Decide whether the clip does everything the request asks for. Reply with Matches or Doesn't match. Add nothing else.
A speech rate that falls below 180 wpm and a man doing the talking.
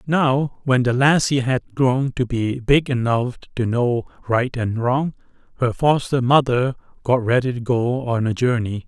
Matches